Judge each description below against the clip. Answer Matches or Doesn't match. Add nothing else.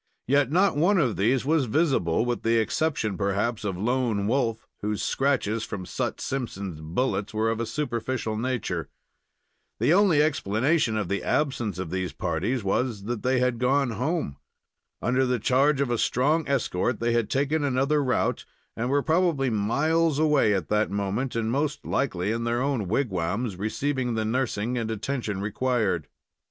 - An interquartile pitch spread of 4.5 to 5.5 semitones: Matches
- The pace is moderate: Matches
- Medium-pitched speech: Doesn't match